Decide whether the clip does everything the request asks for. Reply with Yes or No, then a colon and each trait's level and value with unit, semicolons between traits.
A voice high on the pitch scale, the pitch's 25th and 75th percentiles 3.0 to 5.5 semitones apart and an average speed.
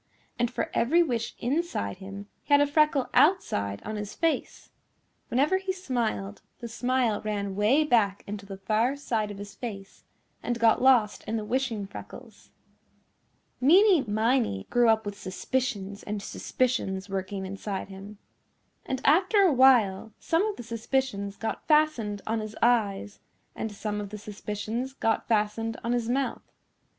Yes: high, 225 Hz; average, 4.4 semitones; average, 155 wpm